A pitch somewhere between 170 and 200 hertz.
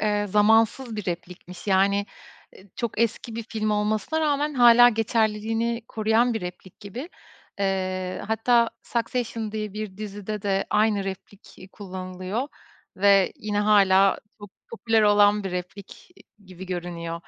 No: high, 210 Hz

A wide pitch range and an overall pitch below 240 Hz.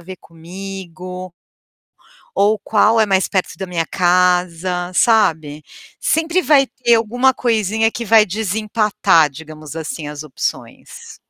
No: average, 4.7 semitones; high, 190 Hz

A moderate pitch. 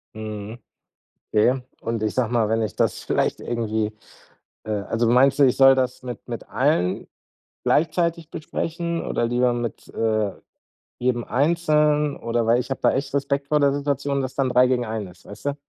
No: low, 125 Hz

